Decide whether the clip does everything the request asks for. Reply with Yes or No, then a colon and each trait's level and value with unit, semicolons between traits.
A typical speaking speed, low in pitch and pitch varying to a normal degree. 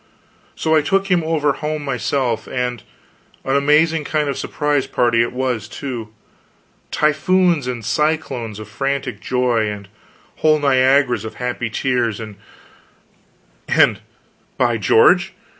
No: slow, 125 wpm; low, 130 Hz; average, 4.3 semitones